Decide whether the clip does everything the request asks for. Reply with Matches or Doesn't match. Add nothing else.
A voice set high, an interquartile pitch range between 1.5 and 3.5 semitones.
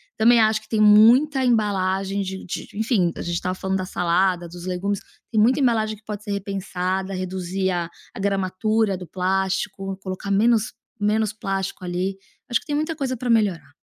Matches